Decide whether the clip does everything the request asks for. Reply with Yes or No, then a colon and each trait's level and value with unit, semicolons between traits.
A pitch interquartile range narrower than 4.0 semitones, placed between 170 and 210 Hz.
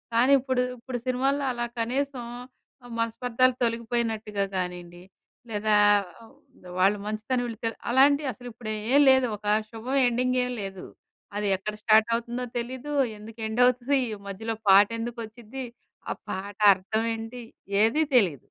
No: average, 2.8 semitones; high, 230 Hz